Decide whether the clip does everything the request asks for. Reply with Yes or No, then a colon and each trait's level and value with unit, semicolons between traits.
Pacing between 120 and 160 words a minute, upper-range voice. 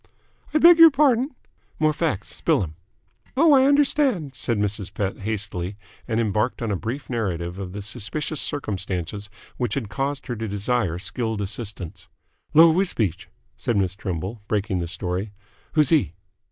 No: average, 155 wpm; low, 110 Hz